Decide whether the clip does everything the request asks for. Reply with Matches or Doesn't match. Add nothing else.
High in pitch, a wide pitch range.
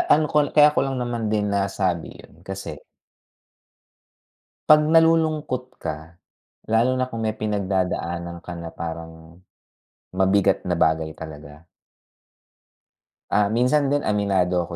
Doesn't match